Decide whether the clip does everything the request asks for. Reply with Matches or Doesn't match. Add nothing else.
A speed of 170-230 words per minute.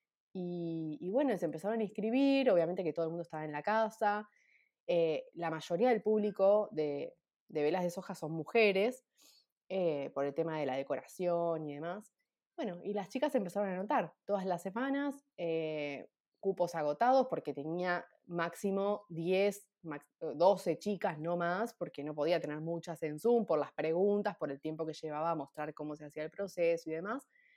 Matches